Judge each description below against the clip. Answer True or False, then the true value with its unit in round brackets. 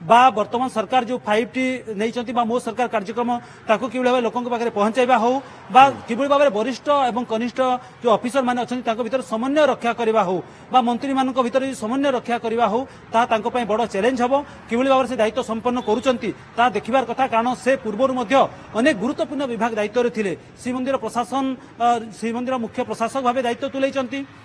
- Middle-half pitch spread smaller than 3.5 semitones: True (2.4 semitones)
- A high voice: True (245 Hz)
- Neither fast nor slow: False (95 wpm)